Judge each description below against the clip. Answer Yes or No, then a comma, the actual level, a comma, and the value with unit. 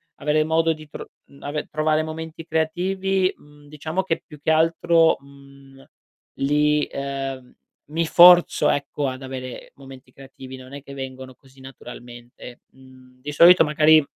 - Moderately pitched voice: Yes, medium, 145 Hz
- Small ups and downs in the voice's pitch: No, average, 3.0 semitones